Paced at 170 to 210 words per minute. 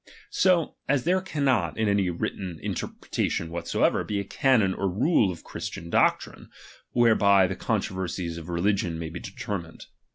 No: average, 155 wpm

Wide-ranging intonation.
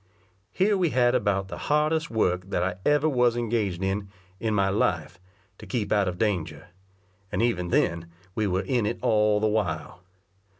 No: average, 4.6 semitones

